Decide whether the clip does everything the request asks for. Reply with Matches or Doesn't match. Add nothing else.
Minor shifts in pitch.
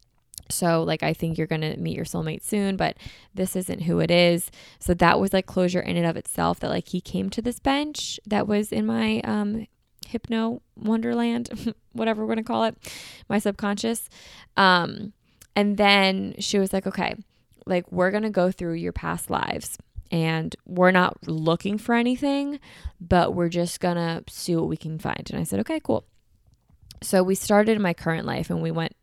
Doesn't match